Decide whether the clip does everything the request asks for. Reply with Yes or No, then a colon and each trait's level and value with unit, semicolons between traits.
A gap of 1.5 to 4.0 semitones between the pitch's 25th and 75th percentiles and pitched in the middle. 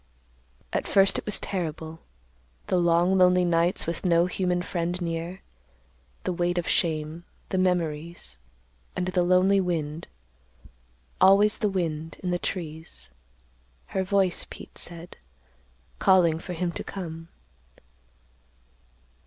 Yes: narrow, 2.4 semitones; medium, 175 Hz